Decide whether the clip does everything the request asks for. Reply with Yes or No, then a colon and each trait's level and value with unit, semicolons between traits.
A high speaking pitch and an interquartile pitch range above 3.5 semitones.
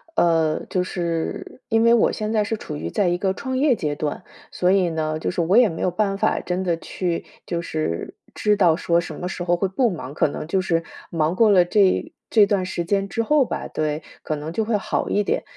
No: medium, 180 Hz; average, 3.9 semitones